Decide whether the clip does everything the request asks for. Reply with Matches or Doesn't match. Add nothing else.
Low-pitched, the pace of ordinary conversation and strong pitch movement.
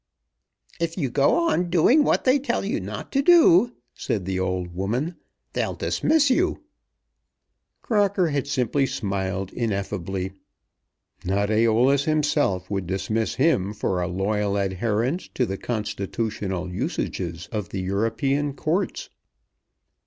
Doesn't match